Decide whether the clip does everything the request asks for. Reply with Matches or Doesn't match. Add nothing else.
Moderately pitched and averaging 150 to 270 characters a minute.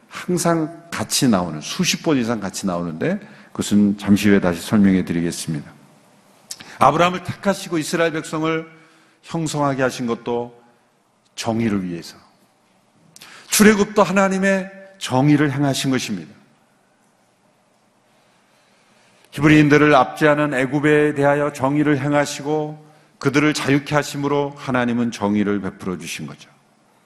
Doesn't match